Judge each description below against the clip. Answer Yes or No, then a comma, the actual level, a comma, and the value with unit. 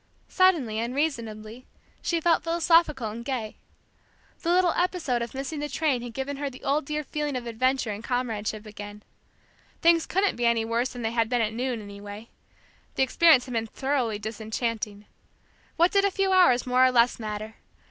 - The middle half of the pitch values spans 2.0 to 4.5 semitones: No, average, 5.2 semitones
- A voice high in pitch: Yes, very high, 250 Hz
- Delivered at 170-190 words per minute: Yes, average, 180 wpm